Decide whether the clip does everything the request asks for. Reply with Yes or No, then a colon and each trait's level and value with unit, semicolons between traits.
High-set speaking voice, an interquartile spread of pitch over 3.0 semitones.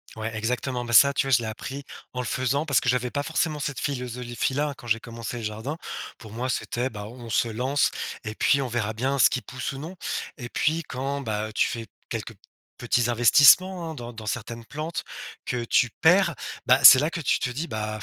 No: low, 125 Hz; average, 3.5 semitones